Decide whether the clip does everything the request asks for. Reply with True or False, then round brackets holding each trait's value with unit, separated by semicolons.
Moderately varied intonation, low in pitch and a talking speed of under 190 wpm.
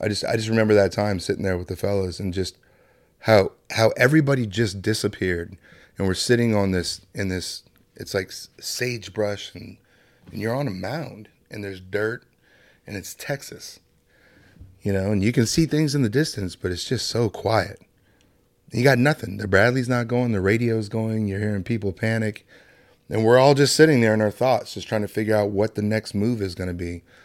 False (3.5 semitones; 105 Hz; 205 wpm)